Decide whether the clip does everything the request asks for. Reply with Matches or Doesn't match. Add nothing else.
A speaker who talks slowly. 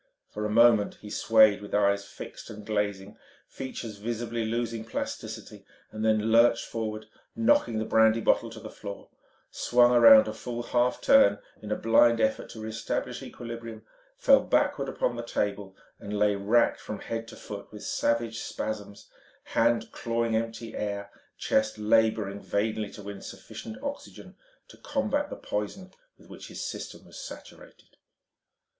Doesn't match